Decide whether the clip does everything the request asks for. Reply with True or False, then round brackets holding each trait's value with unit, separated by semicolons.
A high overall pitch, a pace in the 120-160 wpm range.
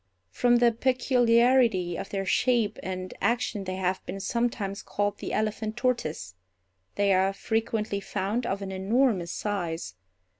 True (205 Hz; 140 wpm)